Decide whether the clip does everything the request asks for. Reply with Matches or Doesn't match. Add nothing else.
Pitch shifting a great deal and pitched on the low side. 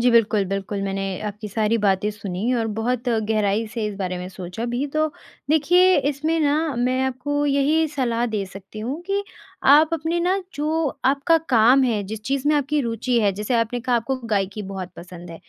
Doesn't match